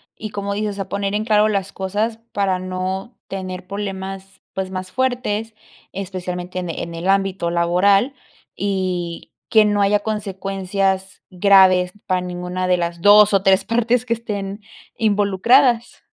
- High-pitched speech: Yes, high, 195 Hz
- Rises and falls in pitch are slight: Yes, narrow, 2.1 semitones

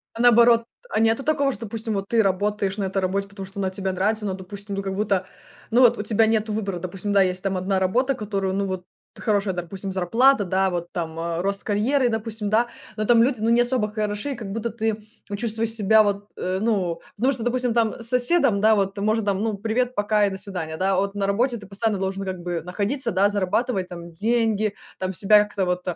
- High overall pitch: Yes, high, 205 Hz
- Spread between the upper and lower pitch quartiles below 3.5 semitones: Yes, average, 2.9 semitones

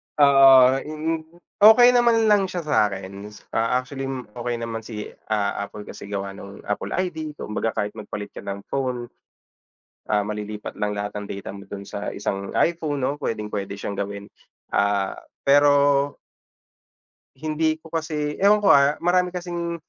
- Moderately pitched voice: No, low, 130 Hz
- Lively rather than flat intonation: Yes, wide, 7.3 semitones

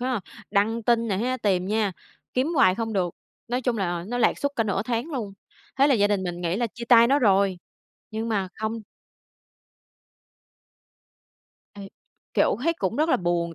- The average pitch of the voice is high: Yes, high, 220 Hz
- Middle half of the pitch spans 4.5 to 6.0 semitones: No, average, 4.0 semitones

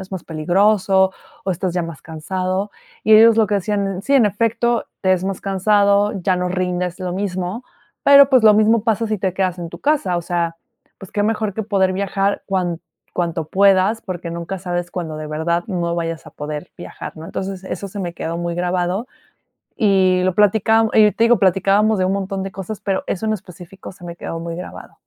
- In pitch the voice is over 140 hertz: Yes, high, 190 Hz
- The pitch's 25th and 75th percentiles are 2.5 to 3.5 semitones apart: Yes, average, 2.8 semitones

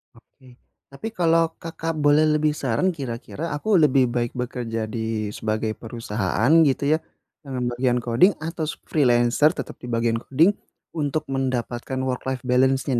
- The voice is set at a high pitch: No, low, 130 Hz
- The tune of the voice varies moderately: Yes, average, 4.2 semitones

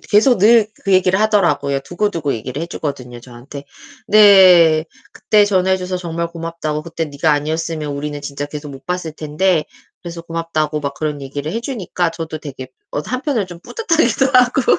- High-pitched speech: No, medium, 165 Hz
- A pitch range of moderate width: Yes, average, 4.5 semitones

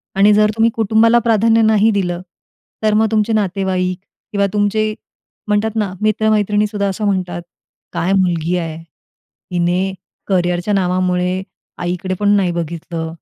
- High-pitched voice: Yes, high, 200 Hz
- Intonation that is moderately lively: Yes, average, 3.0 semitones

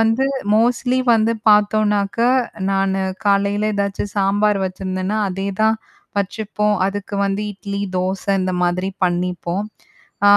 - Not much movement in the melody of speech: Yes, narrow, 1.7 semitones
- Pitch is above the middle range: Yes, high, 200 Hz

